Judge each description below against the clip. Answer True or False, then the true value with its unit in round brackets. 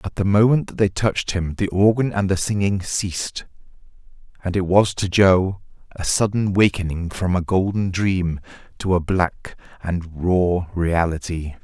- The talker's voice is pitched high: False (95 Hz)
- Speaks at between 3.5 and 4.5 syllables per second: True (4.4 syllables/s)